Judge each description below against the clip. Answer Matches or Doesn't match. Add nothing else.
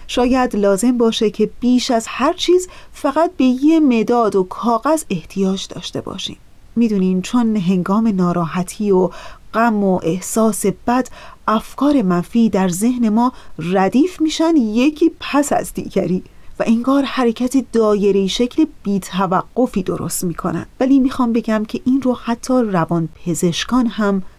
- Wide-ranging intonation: Doesn't match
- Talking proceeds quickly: Doesn't match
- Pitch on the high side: Matches